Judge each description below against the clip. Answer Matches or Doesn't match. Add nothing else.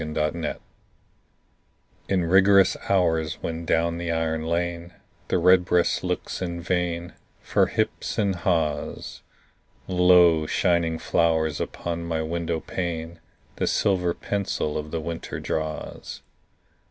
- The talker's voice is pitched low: Matches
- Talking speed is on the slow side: Matches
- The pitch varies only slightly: Matches